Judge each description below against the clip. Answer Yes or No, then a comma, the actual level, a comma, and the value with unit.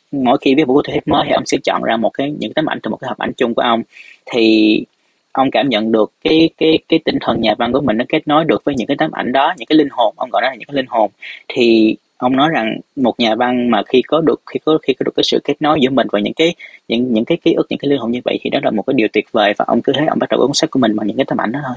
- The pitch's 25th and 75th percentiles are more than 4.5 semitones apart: Yes, average, 5.2 semitones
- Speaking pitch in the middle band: No, low, 130 Hz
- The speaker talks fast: Yes, fast, 340 wpm